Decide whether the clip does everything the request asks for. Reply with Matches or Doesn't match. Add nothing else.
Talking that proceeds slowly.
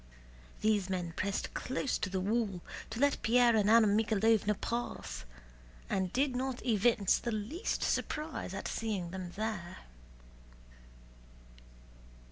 Matches